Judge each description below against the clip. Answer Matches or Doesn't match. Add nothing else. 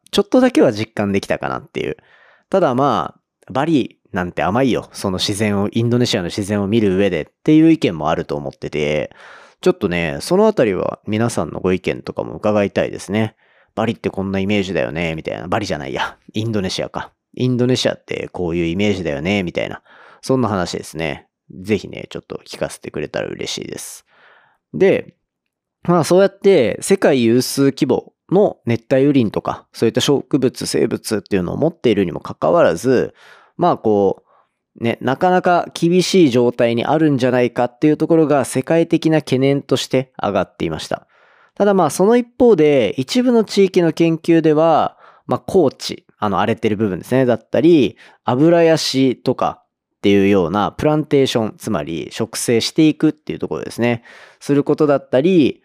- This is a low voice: Matches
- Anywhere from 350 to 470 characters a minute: Matches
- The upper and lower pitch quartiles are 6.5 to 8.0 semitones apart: Matches